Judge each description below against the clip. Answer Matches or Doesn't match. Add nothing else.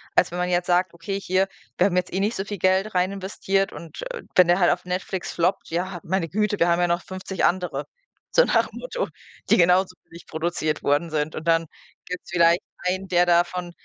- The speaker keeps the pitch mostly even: Matches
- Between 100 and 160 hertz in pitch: Doesn't match